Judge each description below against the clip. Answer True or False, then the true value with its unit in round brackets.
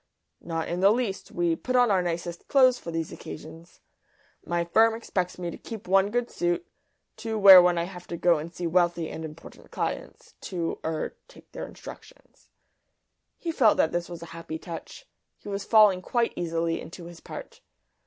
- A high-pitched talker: False (175 Hz)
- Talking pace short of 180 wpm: False (185 wpm)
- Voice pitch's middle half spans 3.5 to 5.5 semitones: True (3.9 semitones)